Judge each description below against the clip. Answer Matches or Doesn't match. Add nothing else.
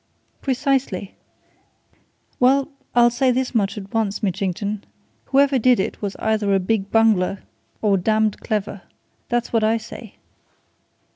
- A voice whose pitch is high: Matches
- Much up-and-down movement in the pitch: Doesn't match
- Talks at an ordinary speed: Doesn't match